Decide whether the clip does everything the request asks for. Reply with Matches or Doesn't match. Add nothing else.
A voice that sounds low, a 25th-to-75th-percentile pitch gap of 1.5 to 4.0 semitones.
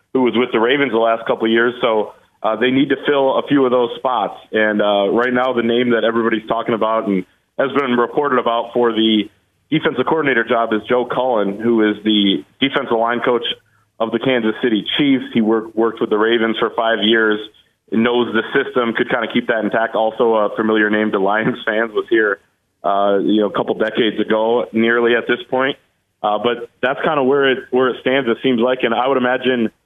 Matches